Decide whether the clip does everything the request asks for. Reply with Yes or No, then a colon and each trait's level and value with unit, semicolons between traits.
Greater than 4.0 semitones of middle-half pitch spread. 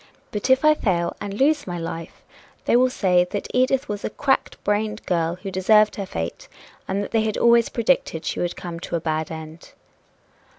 Yes: wide, 5.4 semitones